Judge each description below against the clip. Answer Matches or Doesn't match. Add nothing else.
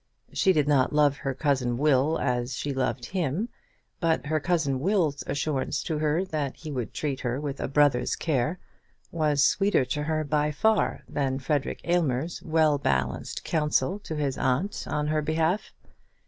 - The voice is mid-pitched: Matches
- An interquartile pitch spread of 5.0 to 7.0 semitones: Doesn't match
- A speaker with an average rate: Matches